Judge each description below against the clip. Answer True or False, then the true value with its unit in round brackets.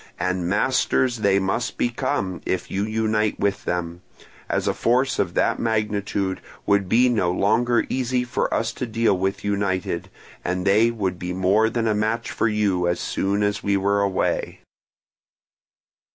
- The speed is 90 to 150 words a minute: False (160 wpm)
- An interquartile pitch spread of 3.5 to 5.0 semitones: False (3.1 semitones)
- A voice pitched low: True (100 Hz)